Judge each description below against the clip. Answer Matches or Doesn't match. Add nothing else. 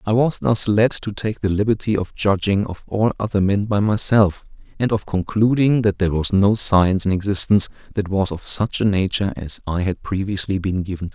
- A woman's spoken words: Doesn't match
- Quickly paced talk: Matches